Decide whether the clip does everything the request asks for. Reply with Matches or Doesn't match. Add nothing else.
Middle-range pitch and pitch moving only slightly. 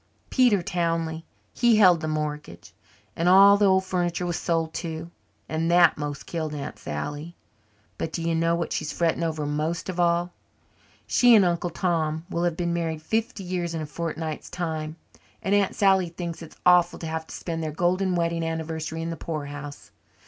Matches